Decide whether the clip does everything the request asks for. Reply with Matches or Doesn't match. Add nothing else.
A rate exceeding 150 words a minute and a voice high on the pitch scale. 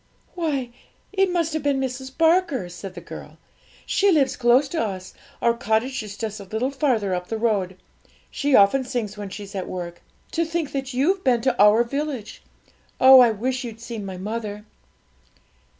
Matches